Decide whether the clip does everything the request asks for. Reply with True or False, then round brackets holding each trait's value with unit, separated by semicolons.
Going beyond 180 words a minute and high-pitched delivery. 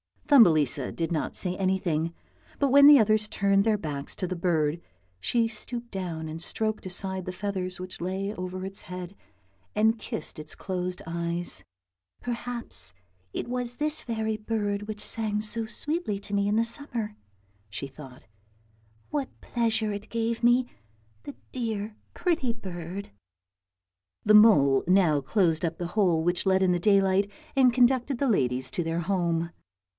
False (165 wpm; 195 Hz)